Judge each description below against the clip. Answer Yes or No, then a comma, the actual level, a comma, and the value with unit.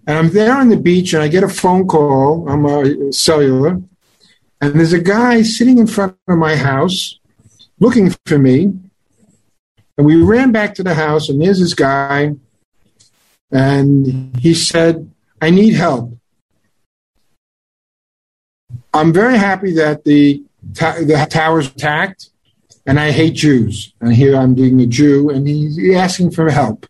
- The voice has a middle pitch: Yes, medium, 155 Hz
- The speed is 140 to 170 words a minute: Yes, average, 155 wpm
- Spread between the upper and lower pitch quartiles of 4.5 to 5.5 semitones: Yes, average, 5.1 semitones